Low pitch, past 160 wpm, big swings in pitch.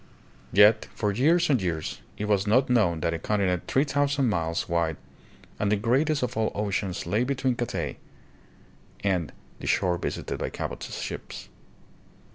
No: low, 105 Hz; average, 155 wpm; wide, 6.0 semitones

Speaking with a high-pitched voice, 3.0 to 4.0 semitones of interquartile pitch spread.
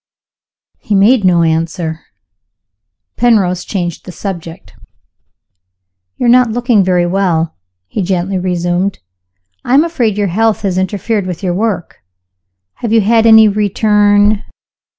Yes: high, 195 Hz; average, 3.7 semitones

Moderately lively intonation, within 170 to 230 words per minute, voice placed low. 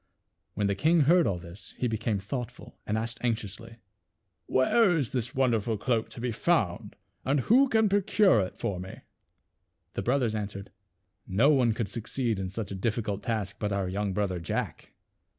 Yes: average, 4.6 semitones; average, 180 wpm; low, 115 Hz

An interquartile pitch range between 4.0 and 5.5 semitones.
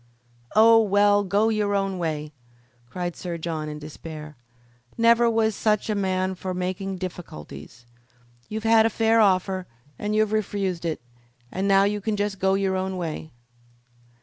No: average, 3.1 semitones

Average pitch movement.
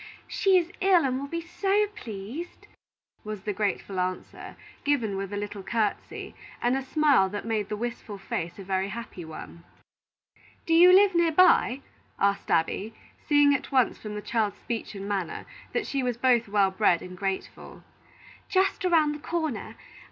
No: wide, 7.4 semitones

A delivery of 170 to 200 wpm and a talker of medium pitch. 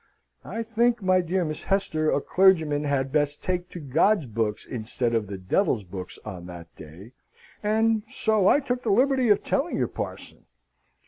Yes: average, 175 wpm; medium, 165 Hz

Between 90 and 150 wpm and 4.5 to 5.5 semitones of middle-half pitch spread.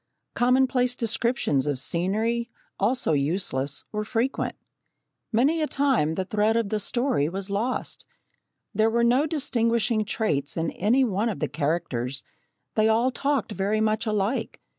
Yes: average, 140 wpm; average, 4.8 semitones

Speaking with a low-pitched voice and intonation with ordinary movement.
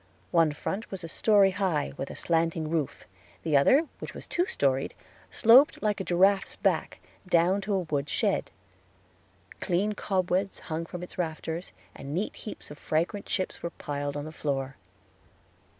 No: medium, 175 Hz; average, 4.2 semitones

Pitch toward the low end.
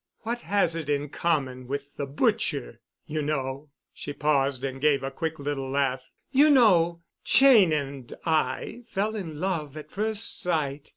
No: medium, 150 Hz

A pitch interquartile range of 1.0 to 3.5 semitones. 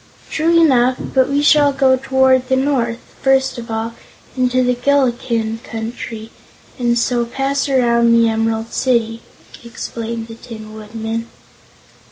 Yes: narrow, 2.5 semitones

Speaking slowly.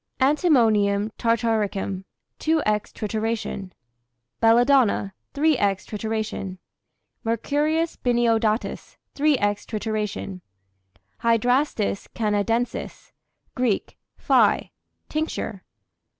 Yes: slow, 60 wpm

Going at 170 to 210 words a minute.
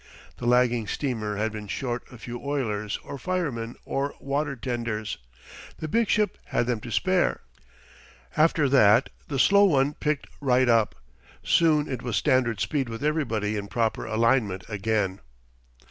No: average, 150 wpm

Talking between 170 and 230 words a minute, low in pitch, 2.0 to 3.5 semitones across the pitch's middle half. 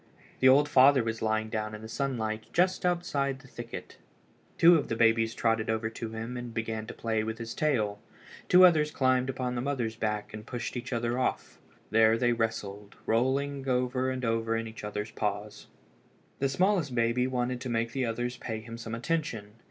Yes: average, 190 wpm; low, 120 Hz; average, 2.8 semitones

